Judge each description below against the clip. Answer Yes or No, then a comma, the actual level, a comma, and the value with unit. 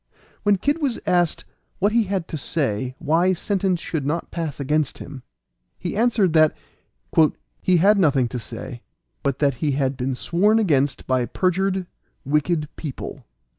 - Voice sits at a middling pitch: Yes, medium, 165 Hz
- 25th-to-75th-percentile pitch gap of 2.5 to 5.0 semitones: No, wide, 5.5 semitones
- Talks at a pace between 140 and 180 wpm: Yes, average, 155 wpm